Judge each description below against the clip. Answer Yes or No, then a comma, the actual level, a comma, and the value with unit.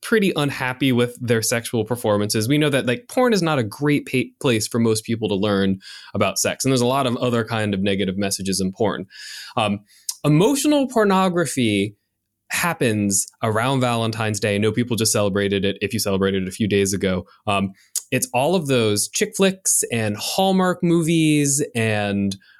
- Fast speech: No, average, 180 wpm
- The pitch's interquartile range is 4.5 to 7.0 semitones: Yes, wide, 5.6 semitones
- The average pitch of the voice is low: Yes, low, 115 Hz